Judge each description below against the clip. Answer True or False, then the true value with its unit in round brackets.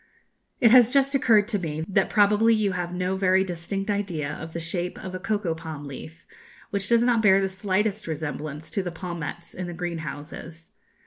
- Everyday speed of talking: True (190 wpm)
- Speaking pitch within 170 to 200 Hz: True (185 Hz)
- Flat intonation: False (3.8 semitones)